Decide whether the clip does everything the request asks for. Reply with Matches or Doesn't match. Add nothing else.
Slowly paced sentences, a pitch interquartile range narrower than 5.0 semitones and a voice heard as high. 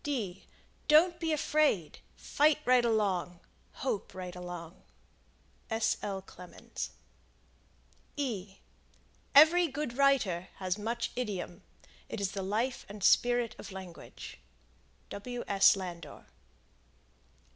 Doesn't match